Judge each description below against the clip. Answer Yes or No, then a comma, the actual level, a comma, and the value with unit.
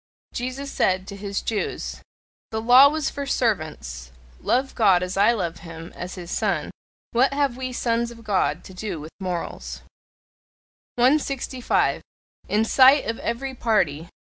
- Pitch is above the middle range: Yes, high, 220 Hz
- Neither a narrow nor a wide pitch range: No, wide, 5.9 semitones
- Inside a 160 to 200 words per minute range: No, average, 145 wpm